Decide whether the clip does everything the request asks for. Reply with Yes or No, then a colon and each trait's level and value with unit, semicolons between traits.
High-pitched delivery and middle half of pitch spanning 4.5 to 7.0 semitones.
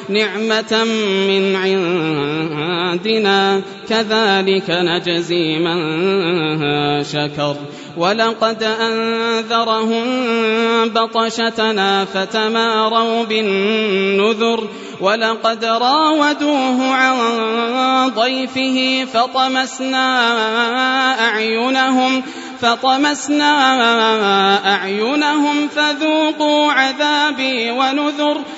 Yes: high, 225 Hz; average, 4.9 semitones